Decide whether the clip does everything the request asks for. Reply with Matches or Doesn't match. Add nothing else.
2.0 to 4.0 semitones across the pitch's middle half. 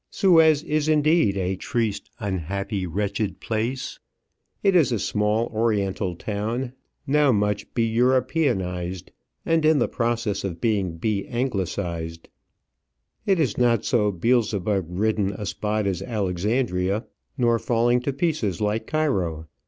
Doesn't match